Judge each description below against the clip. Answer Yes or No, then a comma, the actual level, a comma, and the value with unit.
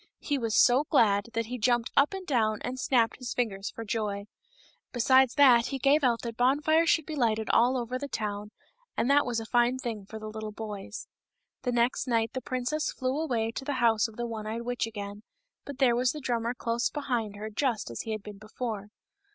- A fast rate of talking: Yes, fast, 215 wpm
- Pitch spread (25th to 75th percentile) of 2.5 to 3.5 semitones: Yes, average, 3.0 semitones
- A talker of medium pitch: No, high, 235 Hz